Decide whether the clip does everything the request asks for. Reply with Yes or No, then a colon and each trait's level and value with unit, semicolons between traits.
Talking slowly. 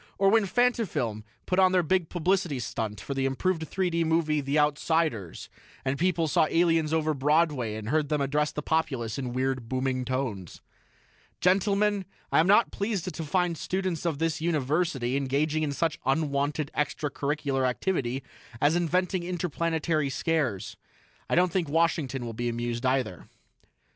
No: average, 160 wpm